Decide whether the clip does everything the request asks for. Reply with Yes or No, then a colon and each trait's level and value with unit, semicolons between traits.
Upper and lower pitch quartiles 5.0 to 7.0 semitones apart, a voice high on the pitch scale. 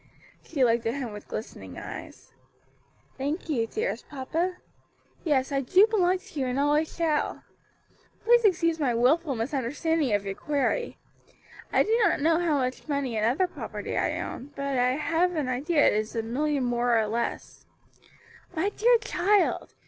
Yes: wide, 5.4 semitones; very high, 290 Hz